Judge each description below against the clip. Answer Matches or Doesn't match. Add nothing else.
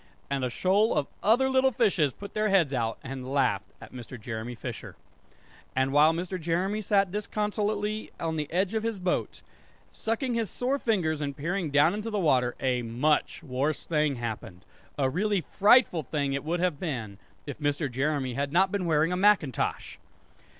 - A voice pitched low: Doesn't match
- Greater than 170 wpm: Matches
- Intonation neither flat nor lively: Doesn't match